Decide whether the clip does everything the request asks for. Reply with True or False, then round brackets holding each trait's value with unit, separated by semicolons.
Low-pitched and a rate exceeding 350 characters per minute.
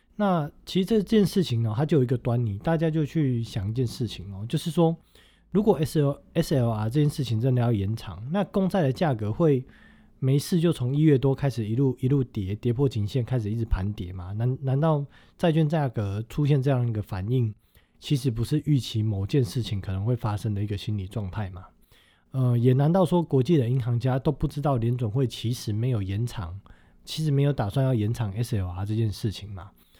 False (125 Hz; 310 characters per minute)